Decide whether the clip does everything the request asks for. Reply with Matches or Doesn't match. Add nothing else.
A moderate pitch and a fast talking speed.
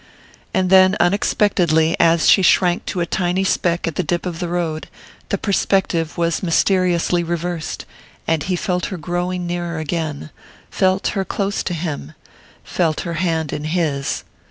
Doesn't match